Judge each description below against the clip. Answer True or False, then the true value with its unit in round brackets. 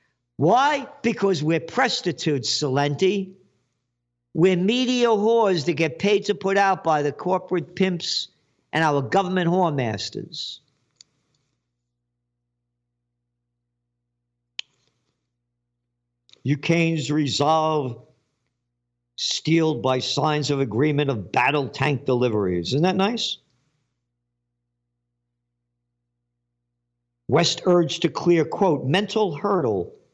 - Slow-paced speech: True (90 wpm)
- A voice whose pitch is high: False (140 Hz)